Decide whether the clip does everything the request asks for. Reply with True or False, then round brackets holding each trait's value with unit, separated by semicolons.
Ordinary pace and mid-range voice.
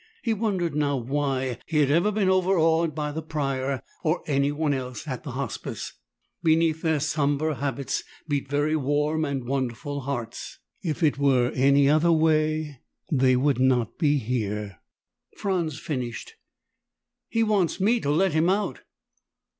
True (145 wpm; 145 Hz)